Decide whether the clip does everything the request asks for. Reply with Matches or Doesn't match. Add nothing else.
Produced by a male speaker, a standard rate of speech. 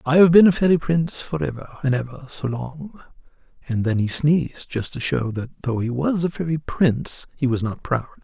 Doesn't match